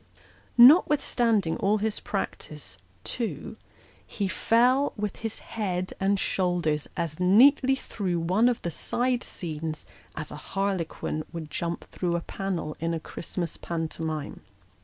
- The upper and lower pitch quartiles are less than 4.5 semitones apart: No, average, 5.2 semitones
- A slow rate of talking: Yes, slow, 130 wpm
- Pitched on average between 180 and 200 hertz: Yes, medium, 185 Hz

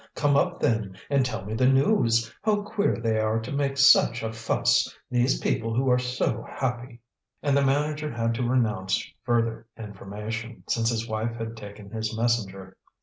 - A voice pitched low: Yes, low, 115 Hz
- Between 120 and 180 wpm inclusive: Yes, average, 175 wpm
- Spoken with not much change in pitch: No, average, 3.0 semitones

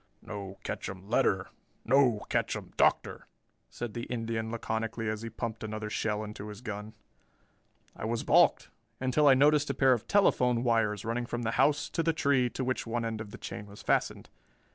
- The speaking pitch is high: No, low, 115 Hz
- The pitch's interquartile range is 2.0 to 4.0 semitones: Yes, average, 2.9 semitones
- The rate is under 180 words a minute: No, average, 185 wpm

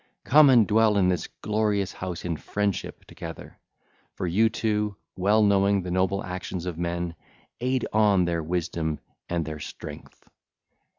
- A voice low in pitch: Yes, very low, 95 Hz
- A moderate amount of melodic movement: Yes, average, 3.4 semitones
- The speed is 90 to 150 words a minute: Yes, average, 145 wpm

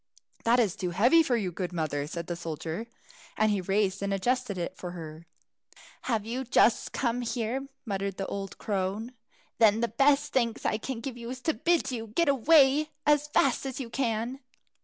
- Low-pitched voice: No, high, 225 Hz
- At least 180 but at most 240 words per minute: Yes, average, 190 wpm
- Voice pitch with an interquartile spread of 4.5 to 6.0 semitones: Yes, average, 5.2 semitones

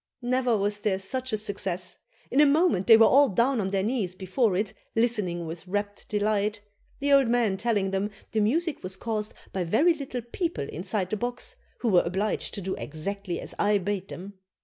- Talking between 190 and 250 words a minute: Yes, average, 195 wpm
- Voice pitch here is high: Yes, high, 210 Hz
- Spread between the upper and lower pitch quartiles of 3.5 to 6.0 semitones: Yes, average, 4.0 semitones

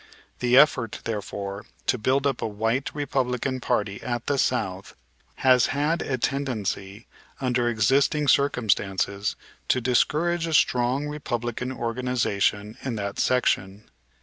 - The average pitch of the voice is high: No, low, 125 Hz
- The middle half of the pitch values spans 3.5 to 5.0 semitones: Yes, average, 4.2 semitones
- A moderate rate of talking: No, slow, 120 wpm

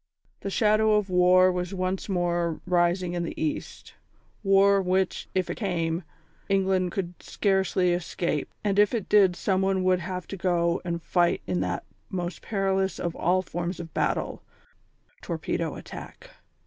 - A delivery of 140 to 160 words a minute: Yes, average, 150 wpm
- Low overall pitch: No, medium, 185 Hz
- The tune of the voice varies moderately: No, narrow, 1.9 semitones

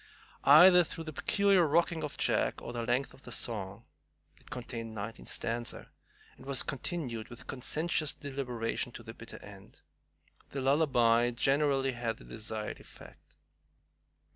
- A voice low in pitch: Yes, low, 125 Hz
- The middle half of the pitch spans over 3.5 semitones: Yes, average, 4.6 semitones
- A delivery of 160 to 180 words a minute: No, average, 140 wpm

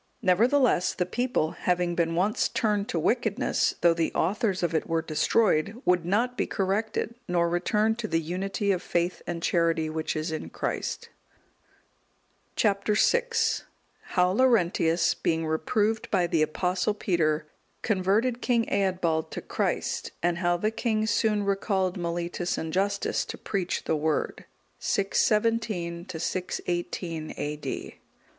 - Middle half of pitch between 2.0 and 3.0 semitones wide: No, average, 4.0 semitones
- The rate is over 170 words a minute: No, slow, 135 wpm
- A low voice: No, medium, 180 Hz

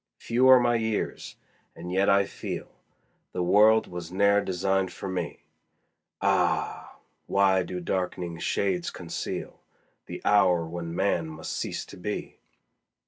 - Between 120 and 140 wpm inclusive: Yes, slow, 135 wpm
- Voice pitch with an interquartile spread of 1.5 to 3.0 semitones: Yes, narrow, 2.4 semitones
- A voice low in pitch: Yes, very low, 95 Hz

